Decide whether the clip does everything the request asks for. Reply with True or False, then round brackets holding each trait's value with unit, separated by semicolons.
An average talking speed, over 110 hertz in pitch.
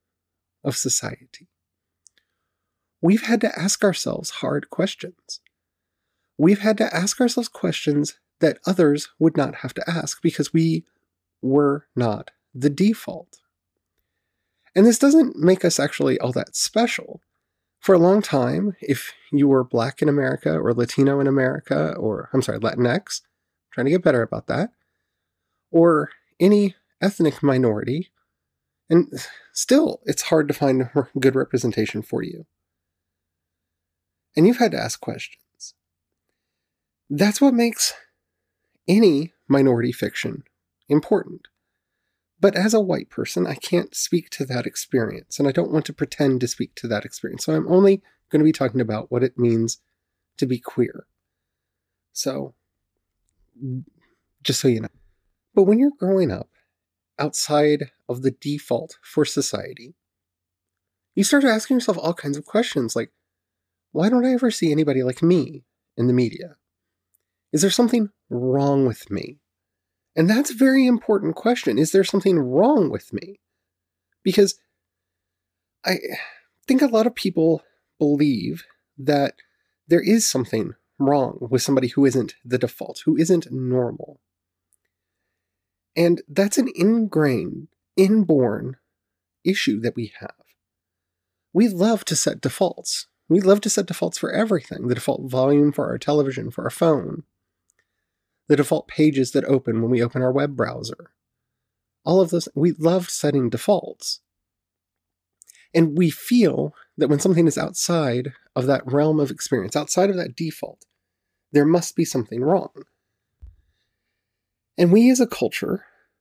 True (145 wpm; 140 Hz)